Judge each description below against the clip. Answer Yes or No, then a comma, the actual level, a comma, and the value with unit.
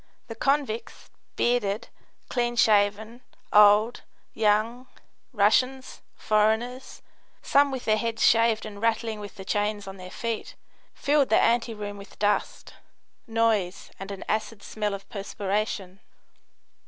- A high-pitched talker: Yes, high, 215 Hz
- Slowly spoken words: Yes, slow, 120 wpm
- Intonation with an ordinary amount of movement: No, narrow, 2.3 semitones